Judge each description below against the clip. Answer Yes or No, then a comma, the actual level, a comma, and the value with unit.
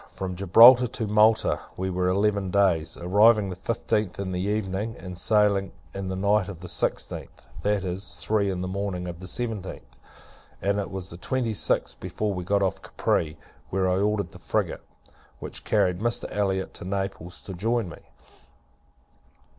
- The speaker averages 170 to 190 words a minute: Yes, average, 175 wpm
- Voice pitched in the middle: No, very low, 95 Hz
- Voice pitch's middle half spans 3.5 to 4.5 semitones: No, narrow, 2.4 semitones